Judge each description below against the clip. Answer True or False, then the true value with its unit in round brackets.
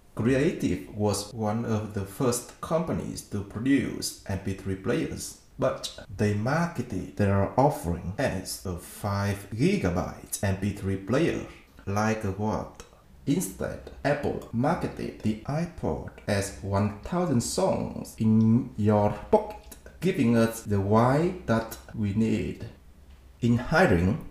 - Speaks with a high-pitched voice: False (105 Hz)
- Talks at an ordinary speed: False (110 wpm)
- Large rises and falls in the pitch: False (2.9 semitones)